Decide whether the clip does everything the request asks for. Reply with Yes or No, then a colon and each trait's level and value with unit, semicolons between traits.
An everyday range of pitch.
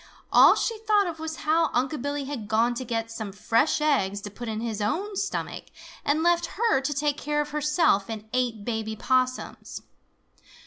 No: wide, 5.8 semitones